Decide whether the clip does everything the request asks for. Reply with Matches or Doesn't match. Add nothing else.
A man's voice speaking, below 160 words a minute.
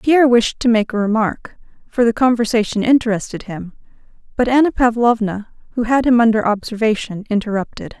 Doesn't match